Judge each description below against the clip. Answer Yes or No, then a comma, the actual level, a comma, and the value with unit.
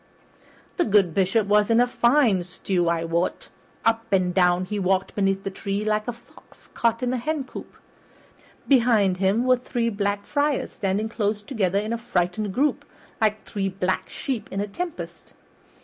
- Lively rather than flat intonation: No, average, 3.6 semitones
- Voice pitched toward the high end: Yes, high, 210 Hz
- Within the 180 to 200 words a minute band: No, average, 170 wpm